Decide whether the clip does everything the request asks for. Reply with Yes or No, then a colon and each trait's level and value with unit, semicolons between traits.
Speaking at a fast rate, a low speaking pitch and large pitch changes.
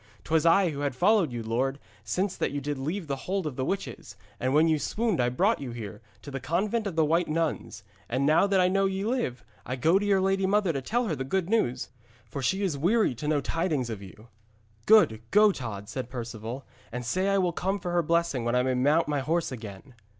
No: fast, 240 wpm; medium, 155 Hz; wide, 6.9 semitones